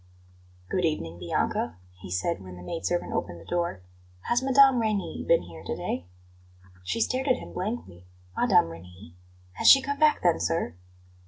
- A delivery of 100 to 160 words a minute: No, average, 170 wpm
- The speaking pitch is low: No, medium, 165 Hz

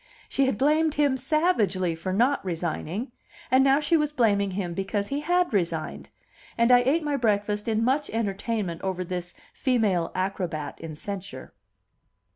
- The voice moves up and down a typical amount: No, wide, 6.7 semitones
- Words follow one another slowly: No, average, 155 wpm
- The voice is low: No, high, 210 Hz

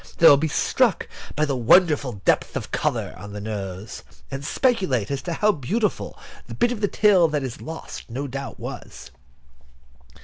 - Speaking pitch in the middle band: Yes, medium, 145 Hz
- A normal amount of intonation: No, wide, 7.5 semitones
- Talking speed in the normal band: Yes, average, 180 wpm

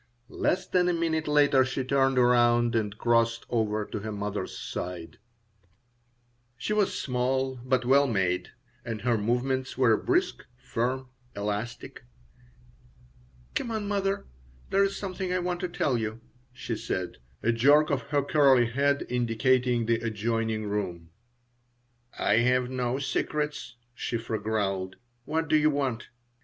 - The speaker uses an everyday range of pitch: Yes, average, 4.1 semitones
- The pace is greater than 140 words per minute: No, slow, 135 wpm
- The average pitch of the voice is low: Yes, low, 125 Hz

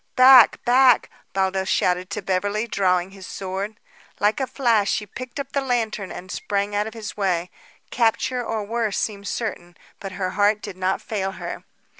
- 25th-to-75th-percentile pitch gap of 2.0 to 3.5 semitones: Yes, average, 3.2 semitones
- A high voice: Yes, high, 205 Hz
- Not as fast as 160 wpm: No, average, 175 wpm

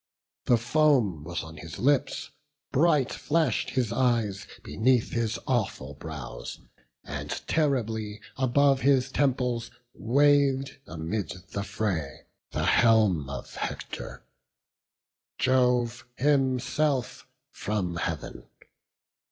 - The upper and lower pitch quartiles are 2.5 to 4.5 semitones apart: No, average, 5.1 semitones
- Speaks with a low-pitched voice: Yes, low, 120 Hz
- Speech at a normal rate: No, slow, 95 wpm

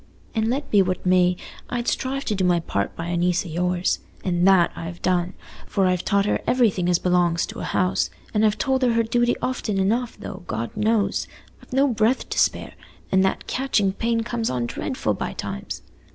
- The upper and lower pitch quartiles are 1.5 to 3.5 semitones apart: No, average, 4.5 semitones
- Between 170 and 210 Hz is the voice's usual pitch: Yes, high, 190 Hz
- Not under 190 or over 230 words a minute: Yes, average, 200 wpm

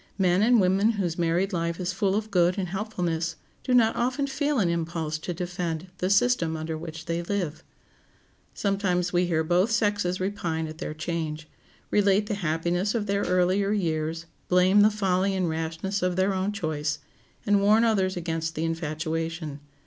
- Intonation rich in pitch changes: No, average, 3.5 semitones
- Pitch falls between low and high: Yes, medium, 180 Hz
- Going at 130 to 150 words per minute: No, average, 170 wpm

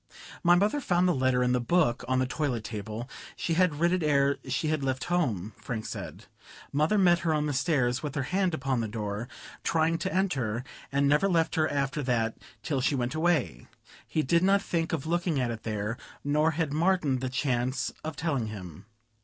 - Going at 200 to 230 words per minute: Yes, fast, 205 wpm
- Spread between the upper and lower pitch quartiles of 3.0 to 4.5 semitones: No, average, 5.0 semitones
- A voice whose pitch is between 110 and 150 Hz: Yes, medium, 140 Hz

